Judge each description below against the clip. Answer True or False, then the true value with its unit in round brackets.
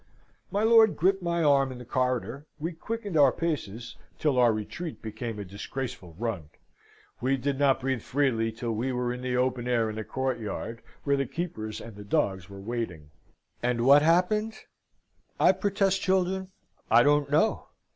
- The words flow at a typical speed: True (170 wpm)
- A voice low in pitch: True (130 Hz)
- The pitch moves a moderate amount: False (5.9 semitones)